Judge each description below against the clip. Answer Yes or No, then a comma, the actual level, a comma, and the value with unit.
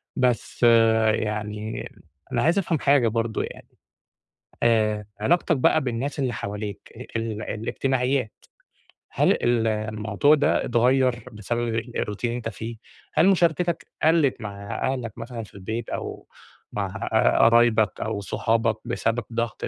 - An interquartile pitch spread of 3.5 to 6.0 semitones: No, average, 3.0 semitones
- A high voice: No, low, 115 Hz